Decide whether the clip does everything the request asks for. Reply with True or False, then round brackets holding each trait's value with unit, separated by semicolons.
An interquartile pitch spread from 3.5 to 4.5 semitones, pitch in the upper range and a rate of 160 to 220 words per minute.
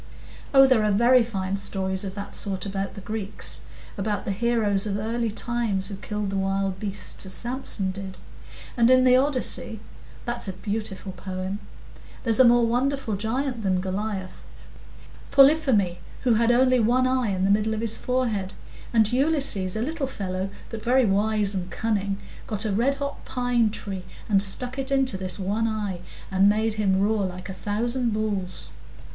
True (3.8 semitones; 215 Hz; 165 wpm)